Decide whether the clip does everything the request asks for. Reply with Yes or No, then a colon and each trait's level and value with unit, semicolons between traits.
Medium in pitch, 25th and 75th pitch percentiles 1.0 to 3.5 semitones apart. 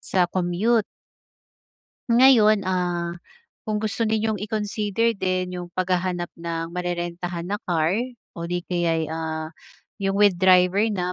Yes: medium, 180 Hz; average, 3.0 semitones